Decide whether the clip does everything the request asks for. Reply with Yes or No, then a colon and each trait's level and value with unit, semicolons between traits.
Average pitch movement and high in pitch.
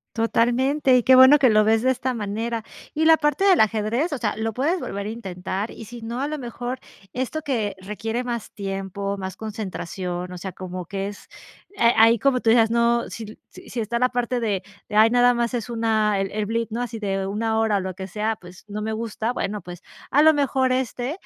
Yes: average, 3.2 semitones; high, 225 Hz